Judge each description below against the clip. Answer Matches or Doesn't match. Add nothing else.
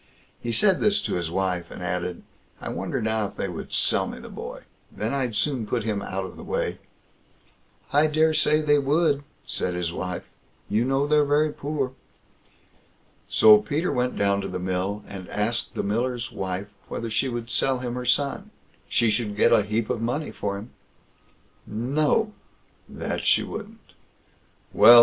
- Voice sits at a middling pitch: Doesn't match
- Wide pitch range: Matches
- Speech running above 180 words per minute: Doesn't match